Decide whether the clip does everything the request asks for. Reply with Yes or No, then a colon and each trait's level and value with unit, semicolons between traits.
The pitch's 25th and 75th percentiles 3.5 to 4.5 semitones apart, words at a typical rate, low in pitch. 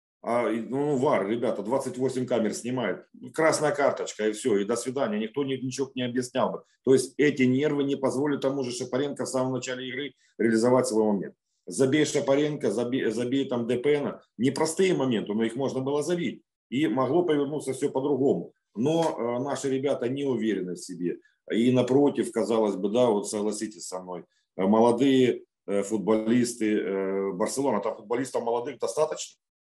No: average, 3.8 semitones; fast, 160 wpm; low, 130 Hz